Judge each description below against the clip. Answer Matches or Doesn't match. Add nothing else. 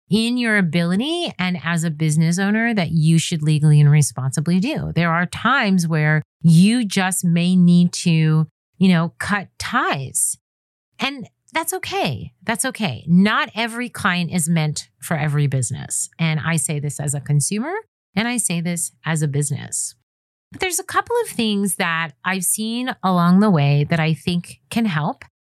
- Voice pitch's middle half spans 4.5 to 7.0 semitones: Matches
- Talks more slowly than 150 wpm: Doesn't match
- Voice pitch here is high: Doesn't match